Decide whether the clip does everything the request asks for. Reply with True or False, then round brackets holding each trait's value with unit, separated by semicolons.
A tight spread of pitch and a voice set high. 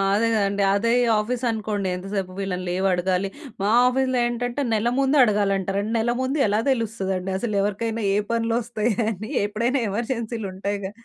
False (3.0 semitones; 215 Hz)